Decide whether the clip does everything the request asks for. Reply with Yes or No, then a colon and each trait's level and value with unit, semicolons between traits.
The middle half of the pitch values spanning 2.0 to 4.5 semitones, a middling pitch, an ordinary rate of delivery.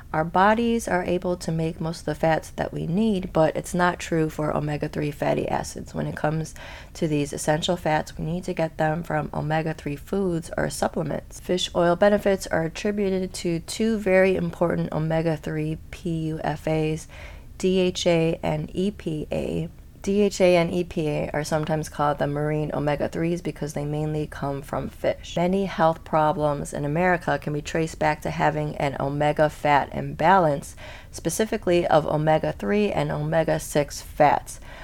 Yes: average, 2.8 semitones; medium, 160 Hz; average, 160 wpm